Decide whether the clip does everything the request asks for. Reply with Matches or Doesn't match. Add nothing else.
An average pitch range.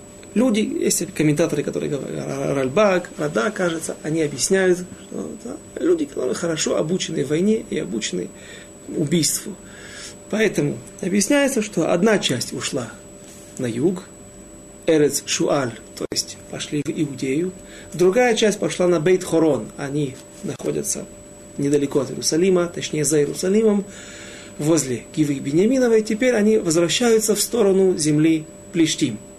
Doesn't match